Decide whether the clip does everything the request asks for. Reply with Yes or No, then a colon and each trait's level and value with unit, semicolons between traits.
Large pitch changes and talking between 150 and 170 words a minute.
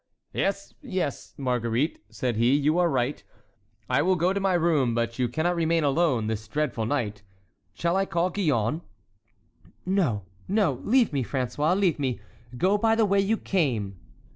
Yes: wide, 7.2 semitones; average, 160 wpm